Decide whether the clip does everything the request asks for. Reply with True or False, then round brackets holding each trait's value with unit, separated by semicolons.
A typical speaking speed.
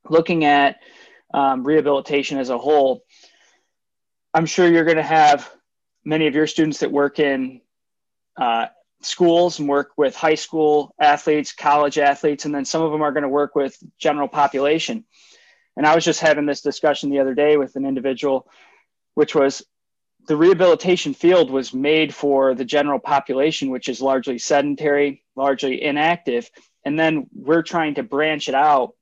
True (165 wpm)